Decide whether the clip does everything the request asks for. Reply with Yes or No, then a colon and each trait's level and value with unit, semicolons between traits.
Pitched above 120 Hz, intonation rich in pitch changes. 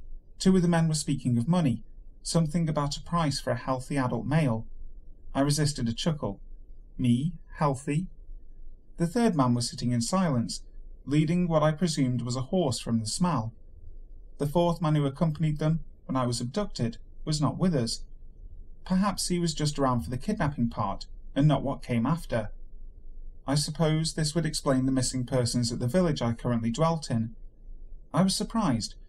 Yes: low, 135 Hz; wide, 5.7 semitones